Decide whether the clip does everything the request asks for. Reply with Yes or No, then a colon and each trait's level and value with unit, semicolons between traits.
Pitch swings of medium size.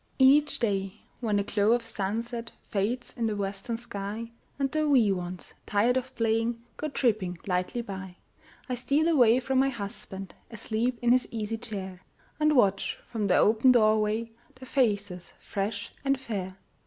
Yes: average, 3.5 semitones